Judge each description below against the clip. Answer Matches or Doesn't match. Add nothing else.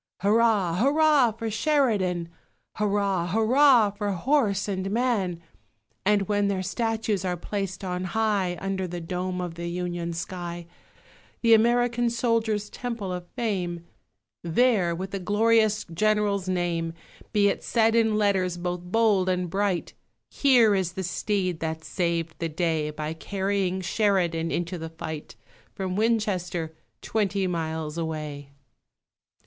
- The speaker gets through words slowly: Matches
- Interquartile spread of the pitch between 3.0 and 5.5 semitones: Matches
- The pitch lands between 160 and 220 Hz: Matches